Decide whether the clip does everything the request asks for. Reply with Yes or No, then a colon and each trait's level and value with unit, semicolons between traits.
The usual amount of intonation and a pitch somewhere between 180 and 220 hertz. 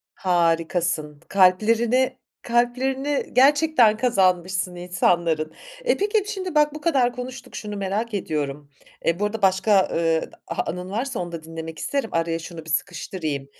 No: wide, 6.9 semitones; high, 190 Hz